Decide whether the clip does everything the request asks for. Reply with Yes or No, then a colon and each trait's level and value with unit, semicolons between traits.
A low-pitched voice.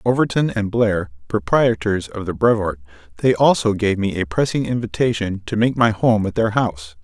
Yes: low, 105 Hz